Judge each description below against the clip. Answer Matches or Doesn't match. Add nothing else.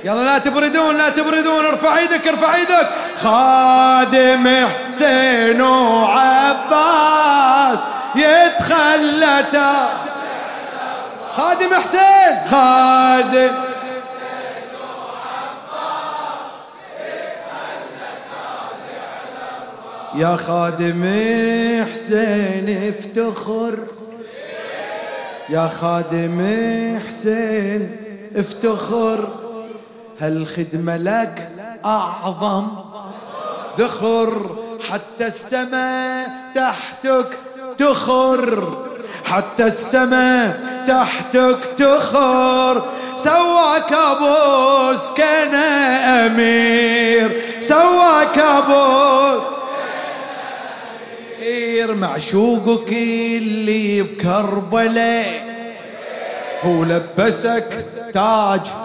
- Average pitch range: Matches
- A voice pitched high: Matches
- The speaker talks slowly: Matches